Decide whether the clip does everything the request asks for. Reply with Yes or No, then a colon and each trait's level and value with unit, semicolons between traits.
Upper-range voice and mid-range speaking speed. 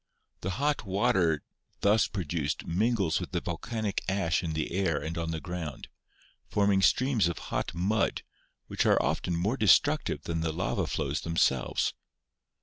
No: very low, 90 Hz; average, 155 wpm